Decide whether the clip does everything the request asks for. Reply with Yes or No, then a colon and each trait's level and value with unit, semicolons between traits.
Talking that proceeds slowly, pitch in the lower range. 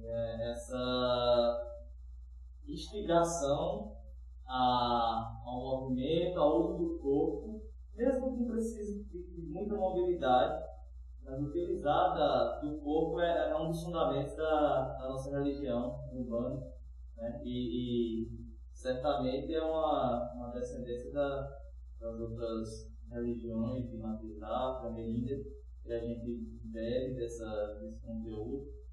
Yes: slow, 105 wpm; low, 120 Hz